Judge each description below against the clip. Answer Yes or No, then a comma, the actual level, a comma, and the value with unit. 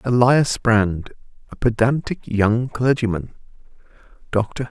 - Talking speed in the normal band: No, slow, 90 wpm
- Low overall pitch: Yes, low, 115 Hz